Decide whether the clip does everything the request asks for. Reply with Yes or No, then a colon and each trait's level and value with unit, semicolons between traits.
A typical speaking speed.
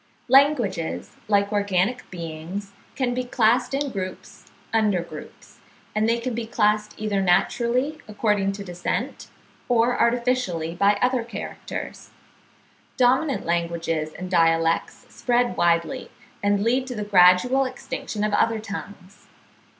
No: slow, 125 wpm